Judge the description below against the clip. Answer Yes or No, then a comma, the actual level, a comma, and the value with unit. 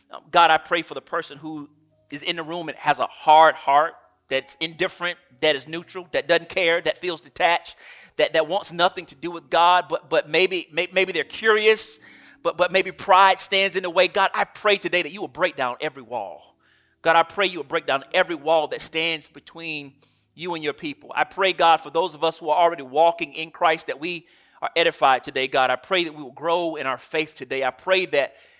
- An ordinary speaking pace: No, fast, 230 wpm